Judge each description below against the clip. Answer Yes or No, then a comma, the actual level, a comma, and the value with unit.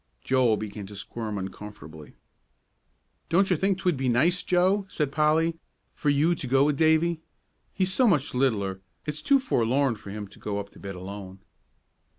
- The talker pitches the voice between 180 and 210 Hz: No, low, 135 Hz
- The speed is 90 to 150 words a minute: No, average, 170 wpm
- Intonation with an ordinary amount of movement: No, wide, 8.3 semitones